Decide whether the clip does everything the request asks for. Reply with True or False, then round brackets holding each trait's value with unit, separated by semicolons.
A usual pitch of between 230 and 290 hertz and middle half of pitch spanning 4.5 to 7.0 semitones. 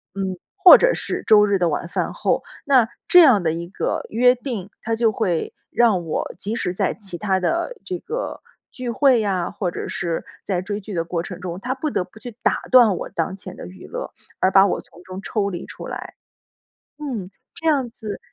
False (205 Hz; 5.4 semitones)